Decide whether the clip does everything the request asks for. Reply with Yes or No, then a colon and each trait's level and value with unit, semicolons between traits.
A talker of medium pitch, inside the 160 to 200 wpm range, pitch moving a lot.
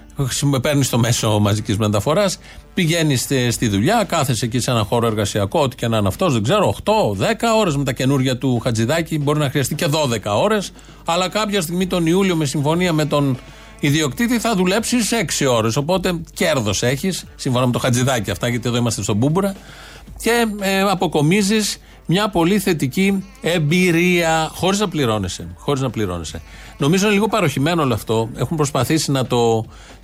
Yes: medium, 145 Hz; average, 165 wpm; wide, 7.0 semitones